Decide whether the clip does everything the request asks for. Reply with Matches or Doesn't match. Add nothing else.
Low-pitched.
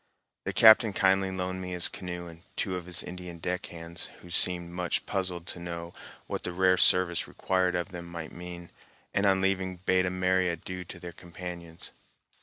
Matches